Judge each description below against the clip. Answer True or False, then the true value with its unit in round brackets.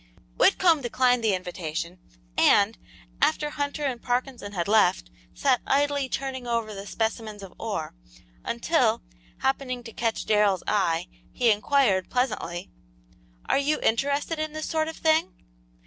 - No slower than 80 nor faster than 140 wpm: True (135 wpm)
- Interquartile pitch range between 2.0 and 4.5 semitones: False (5.6 semitones)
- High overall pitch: True (240 Hz)